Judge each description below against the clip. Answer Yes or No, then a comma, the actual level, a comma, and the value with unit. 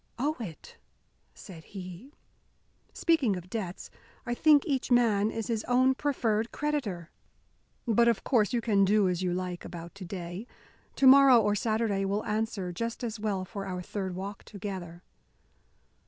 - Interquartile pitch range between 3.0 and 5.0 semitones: Yes, average, 4.3 semitones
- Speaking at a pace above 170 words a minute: No, average, 155 wpm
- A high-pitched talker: Yes, high, 210 Hz